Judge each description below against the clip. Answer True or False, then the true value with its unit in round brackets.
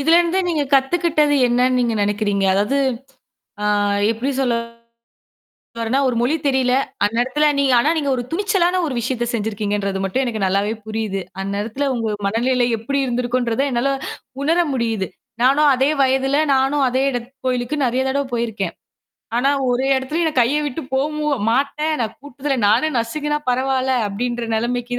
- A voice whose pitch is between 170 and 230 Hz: False (255 Hz)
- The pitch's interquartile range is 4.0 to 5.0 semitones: False (3.5 semitones)